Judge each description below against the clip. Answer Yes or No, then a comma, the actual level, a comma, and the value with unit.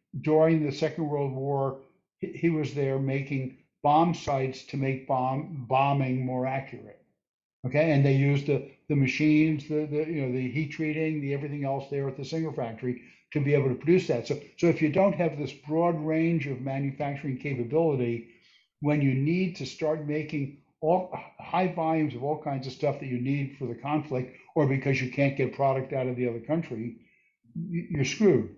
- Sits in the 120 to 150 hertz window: Yes, medium, 140 Hz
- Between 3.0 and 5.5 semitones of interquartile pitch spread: No, narrow, 2.5 semitones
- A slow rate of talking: No, average, 190 wpm